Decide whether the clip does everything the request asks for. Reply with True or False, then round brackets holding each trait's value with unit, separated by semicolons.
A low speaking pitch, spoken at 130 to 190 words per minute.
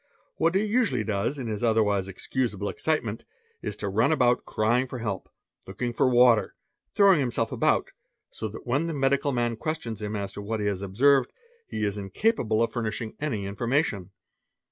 True (115 Hz; 180 wpm)